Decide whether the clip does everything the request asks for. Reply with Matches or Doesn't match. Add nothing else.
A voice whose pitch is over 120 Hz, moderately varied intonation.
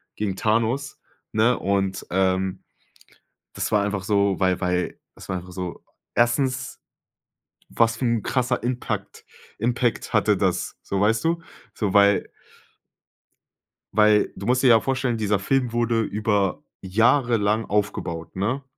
Doesn't match